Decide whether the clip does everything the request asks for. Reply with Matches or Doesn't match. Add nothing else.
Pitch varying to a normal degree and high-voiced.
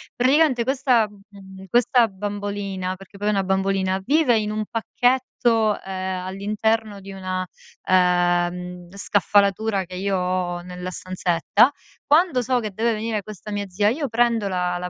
Matches